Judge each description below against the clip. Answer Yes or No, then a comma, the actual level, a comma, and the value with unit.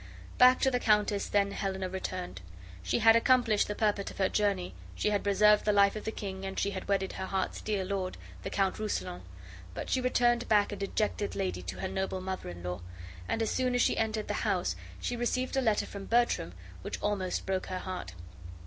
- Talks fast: Yes, fast, 210 wpm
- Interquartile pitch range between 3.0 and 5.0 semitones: No, narrow, 2.6 semitones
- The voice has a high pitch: Yes, high, 200 Hz